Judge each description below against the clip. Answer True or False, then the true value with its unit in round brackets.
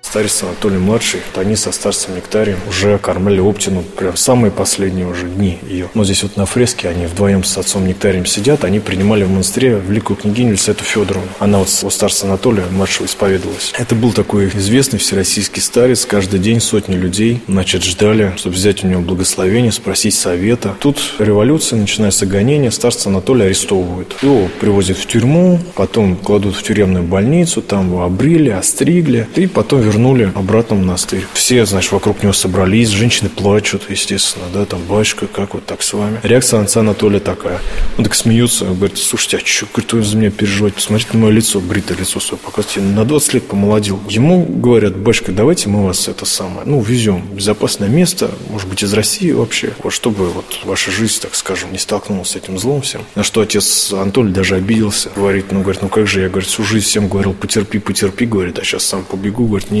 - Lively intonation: False (2.6 semitones)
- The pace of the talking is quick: True (190 wpm)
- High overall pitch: False (100 Hz)